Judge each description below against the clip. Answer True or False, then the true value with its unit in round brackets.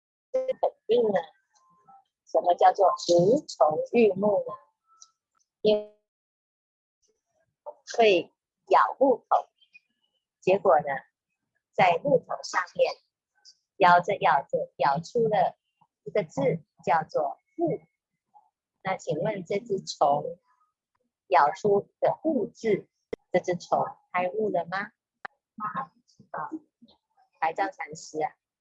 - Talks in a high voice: True (235 Hz)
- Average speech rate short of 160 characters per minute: True (135 characters per minute)